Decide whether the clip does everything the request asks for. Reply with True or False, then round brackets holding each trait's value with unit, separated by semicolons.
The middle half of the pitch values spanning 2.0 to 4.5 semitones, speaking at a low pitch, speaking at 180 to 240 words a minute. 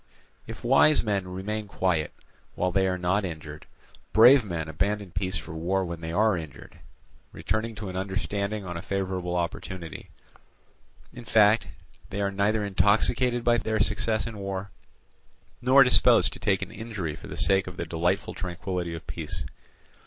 False (3.4 semitones; 95 Hz; 160 wpm)